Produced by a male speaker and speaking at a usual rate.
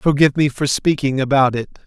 Yes: male; average, 195 wpm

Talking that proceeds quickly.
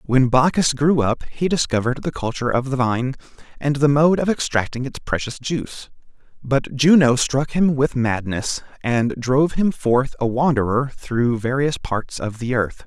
No: average, 175 wpm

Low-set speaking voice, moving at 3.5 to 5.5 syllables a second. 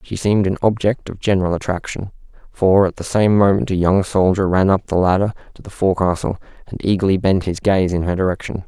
No: very low, 95 Hz; 6.0 syllables/s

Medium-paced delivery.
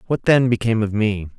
No: fast, 215 wpm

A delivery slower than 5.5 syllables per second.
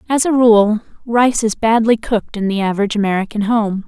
No: 5.8 syllables/s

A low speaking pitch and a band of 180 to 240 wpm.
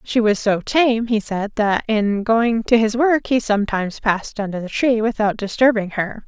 No: high, 220 Hz; average, 200 wpm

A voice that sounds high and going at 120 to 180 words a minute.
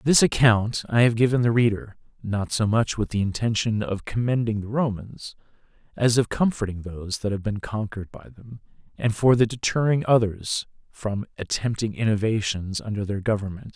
No: low, 110 Hz; average, 165 wpm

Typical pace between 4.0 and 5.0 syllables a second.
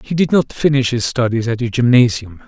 No: 5.6 syllables/s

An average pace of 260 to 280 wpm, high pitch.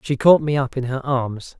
No: fast, 265 wpm; low, 135 Hz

